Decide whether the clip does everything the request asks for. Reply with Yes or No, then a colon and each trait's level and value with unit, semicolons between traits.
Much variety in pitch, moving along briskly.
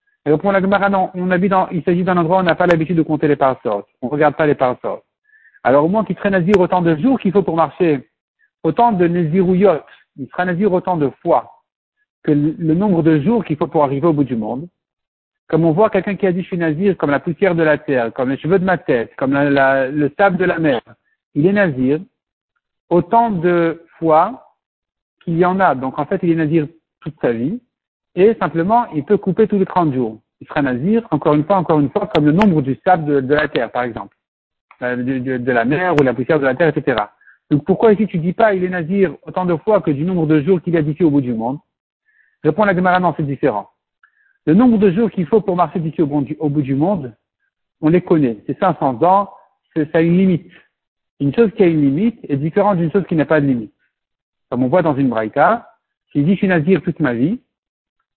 No: average, 4.6 semitones; fast, 245 wpm